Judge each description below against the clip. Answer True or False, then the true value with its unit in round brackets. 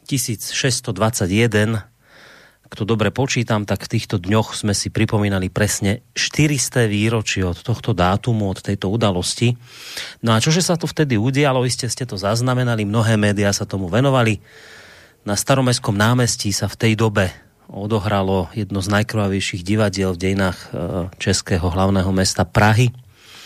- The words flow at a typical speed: True (140 wpm)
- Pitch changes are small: False (3.2 semitones)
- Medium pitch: False (110 Hz)